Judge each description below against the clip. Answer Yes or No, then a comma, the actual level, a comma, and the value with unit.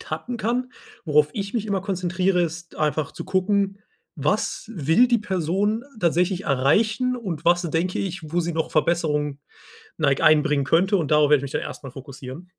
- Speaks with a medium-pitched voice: Yes, medium, 175 Hz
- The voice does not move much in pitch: No, average, 4.6 semitones